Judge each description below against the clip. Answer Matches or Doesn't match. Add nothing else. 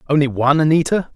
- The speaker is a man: Matches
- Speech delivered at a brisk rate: Doesn't match